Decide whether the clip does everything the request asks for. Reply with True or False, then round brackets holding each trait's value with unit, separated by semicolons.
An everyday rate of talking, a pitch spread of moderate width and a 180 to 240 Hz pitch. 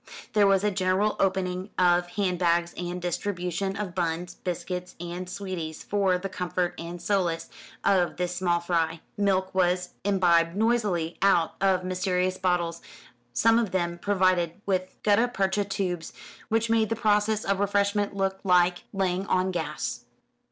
False (150 wpm; 2.1 semitones; 185 Hz)